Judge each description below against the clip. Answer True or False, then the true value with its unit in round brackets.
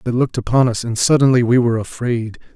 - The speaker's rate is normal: False (235 wpm)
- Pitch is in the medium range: False (120 Hz)